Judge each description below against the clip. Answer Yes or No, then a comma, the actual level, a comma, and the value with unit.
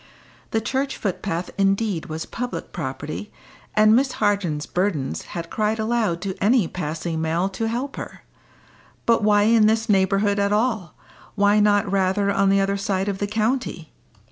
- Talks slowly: No, average, 160 wpm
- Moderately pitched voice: No, high, 200 Hz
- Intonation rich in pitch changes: No, average, 3.0 semitones